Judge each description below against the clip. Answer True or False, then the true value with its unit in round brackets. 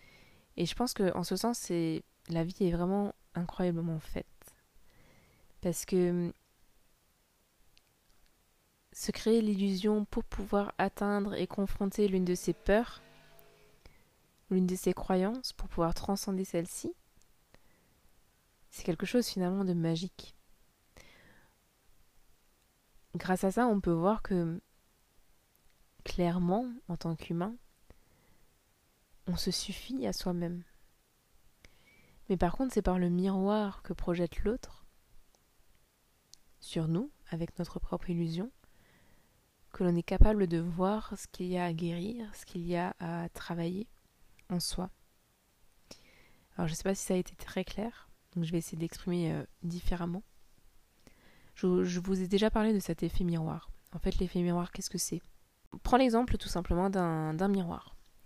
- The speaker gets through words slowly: True (140 wpm)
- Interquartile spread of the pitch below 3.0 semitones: True (2.6 semitones)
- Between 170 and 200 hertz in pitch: True (185 Hz)